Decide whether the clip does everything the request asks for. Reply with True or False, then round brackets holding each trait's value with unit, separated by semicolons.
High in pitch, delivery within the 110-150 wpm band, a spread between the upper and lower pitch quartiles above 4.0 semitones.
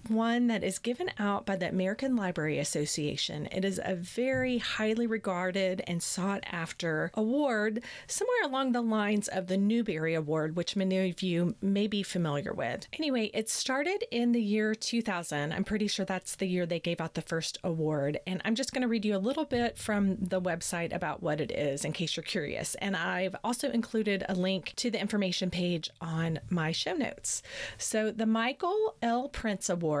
False (195 Hz; 190 wpm; 4.7 semitones)